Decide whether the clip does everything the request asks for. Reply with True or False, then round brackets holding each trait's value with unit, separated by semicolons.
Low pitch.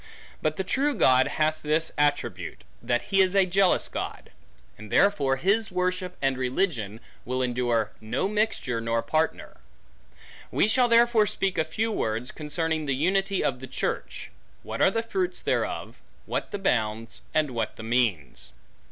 False (155 Hz)